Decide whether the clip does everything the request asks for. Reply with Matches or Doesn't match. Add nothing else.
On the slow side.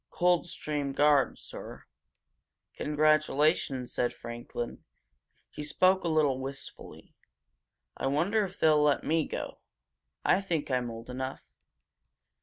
Matches